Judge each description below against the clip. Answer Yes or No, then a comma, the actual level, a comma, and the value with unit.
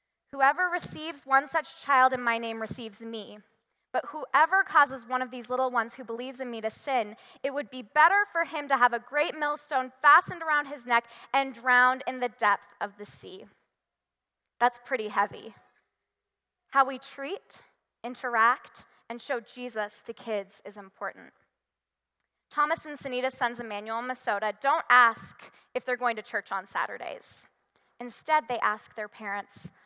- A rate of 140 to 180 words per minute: Yes, average, 165 wpm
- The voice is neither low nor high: No, very high, 250 Hz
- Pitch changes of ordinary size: Yes, average, 3.5 semitones